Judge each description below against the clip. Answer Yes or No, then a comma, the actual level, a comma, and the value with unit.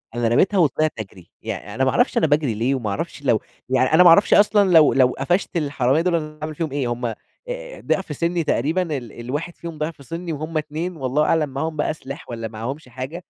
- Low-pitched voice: No, medium, 150 Hz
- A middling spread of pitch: Yes, average, 4.5 semitones